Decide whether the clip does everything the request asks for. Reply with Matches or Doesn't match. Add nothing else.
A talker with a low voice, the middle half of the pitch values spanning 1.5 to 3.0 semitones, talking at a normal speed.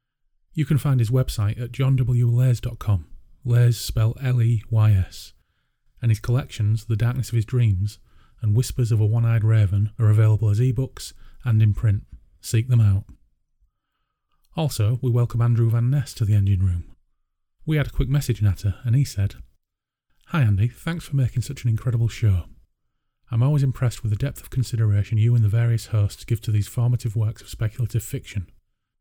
Matches